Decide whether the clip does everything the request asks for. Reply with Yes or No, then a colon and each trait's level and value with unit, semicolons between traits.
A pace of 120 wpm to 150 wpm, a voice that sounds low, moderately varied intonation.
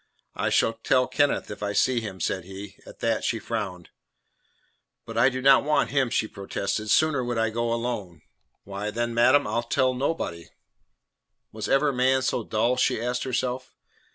No: average, 175 wpm; low, 120 Hz; average, 3.5 semitones